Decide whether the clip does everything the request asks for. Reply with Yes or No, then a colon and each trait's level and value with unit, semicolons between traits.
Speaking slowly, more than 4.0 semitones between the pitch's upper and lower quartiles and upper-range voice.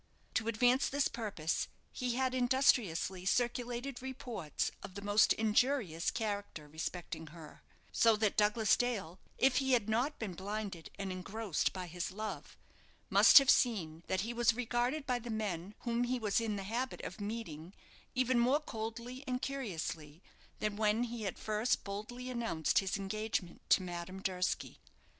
No: average, 155 wpm; average, 4.4 semitones; high, 220 Hz